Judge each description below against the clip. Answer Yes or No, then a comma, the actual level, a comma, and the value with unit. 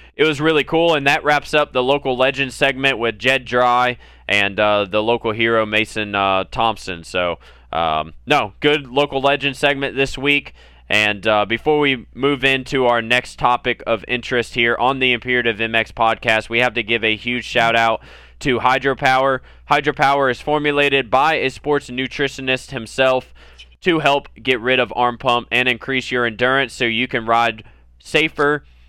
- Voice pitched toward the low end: Yes, low, 125 Hz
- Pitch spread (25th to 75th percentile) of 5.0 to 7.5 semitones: No, average, 3.3 semitones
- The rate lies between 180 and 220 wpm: No, average, 170 wpm